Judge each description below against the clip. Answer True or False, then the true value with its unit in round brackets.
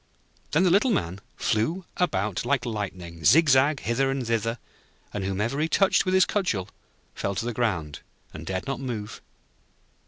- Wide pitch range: True (6.8 semitones)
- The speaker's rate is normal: True (165 wpm)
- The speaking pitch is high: False (115 Hz)